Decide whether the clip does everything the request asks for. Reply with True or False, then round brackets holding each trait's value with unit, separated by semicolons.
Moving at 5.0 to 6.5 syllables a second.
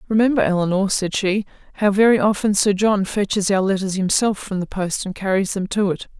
True (5.6 syllables/s)